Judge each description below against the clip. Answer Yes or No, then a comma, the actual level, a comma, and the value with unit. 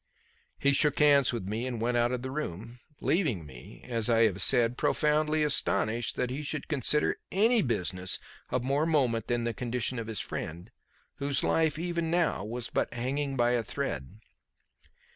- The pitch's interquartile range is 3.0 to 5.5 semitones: Yes, average, 4.5 semitones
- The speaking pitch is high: No, low, 125 Hz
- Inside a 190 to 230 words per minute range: No, average, 175 wpm